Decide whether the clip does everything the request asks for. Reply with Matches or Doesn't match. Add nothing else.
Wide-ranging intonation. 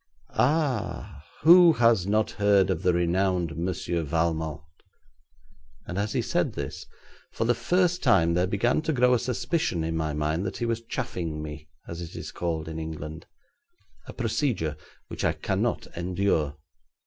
Matches